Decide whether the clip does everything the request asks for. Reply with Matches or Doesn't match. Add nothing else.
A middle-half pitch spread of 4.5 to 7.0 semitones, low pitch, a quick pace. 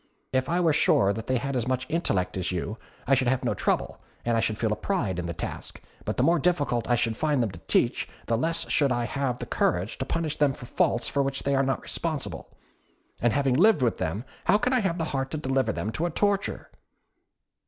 Matches